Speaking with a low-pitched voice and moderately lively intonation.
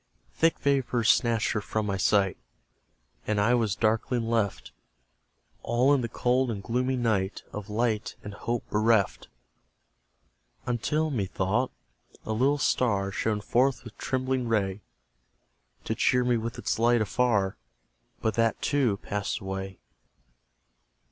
Yes: low, 115 Hz; average, 3.3 semitones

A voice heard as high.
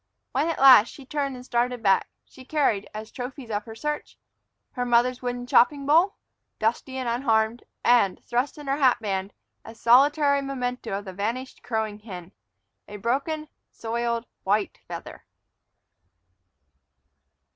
Yes: high, 245 Hz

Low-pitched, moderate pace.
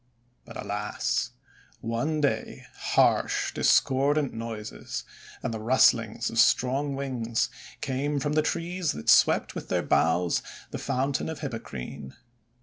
No: low, 125 Hz; slow, 125 wpm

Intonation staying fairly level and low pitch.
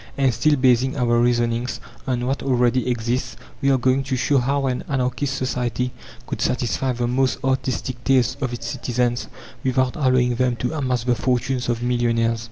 Yes: narrow, 1.5 semitones; low, 125 Hz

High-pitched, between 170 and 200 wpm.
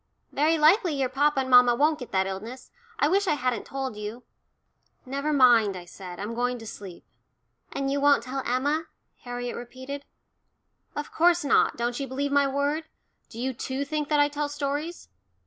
Yes: very high, 270 Hz; average, 180 wpm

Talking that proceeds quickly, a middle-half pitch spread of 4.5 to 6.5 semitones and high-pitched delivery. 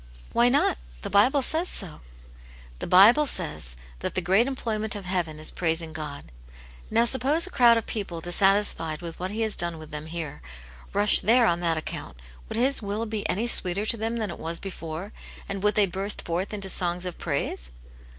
Yes: fast, 210 wpm; average, 5.0 semitones; high, 195 Hz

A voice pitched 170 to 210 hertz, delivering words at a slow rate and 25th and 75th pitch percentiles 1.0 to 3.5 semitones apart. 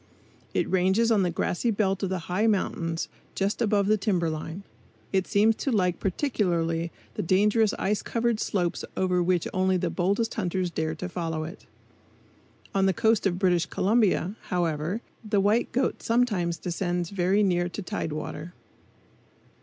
No: high, 190 Hz; average, 160 wpm; average, 3.2 semitones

